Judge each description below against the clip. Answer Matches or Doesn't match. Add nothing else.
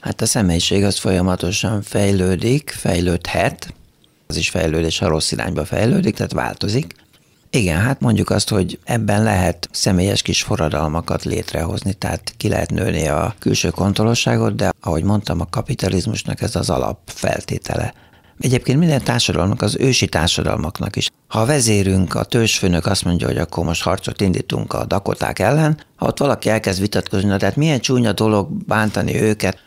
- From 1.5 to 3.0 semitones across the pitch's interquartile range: Doesn't match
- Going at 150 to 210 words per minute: Matches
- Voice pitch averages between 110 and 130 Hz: Doesn't match